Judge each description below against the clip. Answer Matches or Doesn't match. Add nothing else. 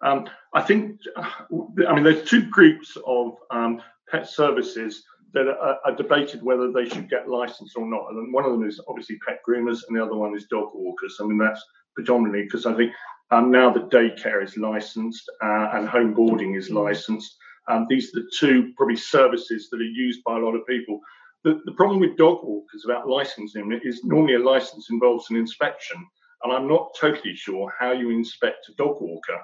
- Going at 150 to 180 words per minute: Doesn't match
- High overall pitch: Doesn't match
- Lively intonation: Doesn't match